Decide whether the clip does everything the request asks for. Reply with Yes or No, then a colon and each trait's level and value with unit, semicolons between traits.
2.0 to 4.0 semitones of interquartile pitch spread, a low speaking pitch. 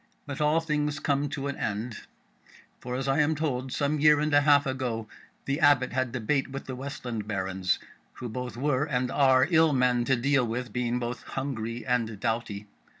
Yes: average, 3.1 semitones; low, 130 Hz